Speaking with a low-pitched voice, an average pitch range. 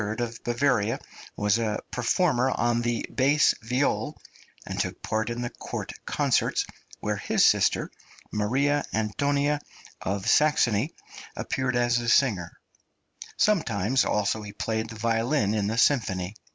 Yes: low, 120 Hz; average, 3.7 semitones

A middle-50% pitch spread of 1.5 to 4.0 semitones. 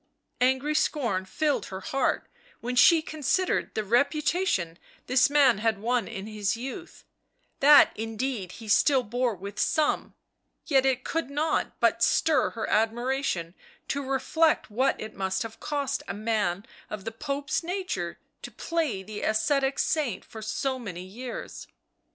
No: average, 5.1 semitones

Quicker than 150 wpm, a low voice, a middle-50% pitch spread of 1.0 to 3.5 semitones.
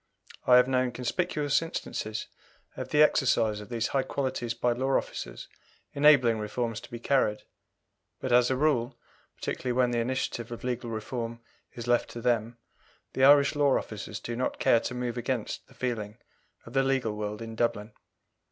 Yes: average, 170 wpm; low, 120 Hz; narrow, 2.4 semitones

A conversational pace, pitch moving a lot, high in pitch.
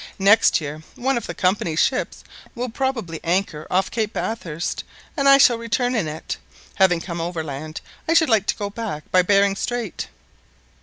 Yes: average, 170 wpm; wide, 6.0 semitones; high, 200 Hz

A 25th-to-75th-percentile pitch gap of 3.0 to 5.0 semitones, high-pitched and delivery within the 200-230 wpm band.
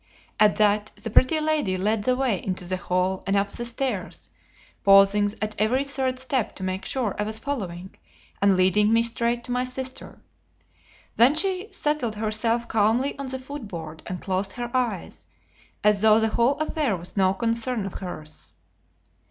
No: average, 4.6 semitones; high, 220 Hz; average, 175 wpm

